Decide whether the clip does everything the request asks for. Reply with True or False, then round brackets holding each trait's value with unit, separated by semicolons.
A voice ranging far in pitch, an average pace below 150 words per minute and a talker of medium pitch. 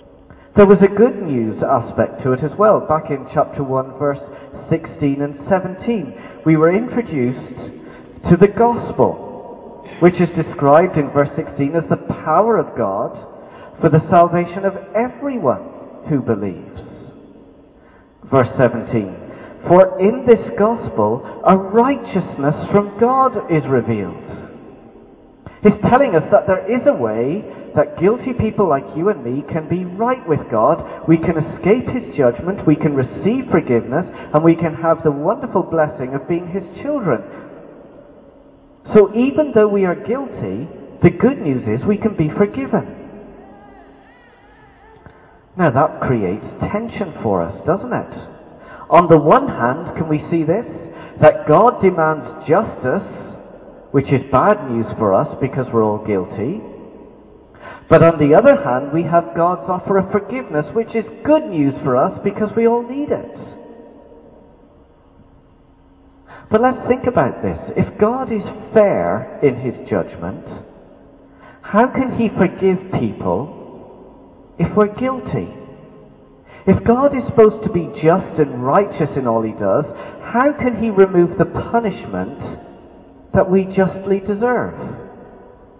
True (6.6 semitones; 140 wpm; 175 Hz)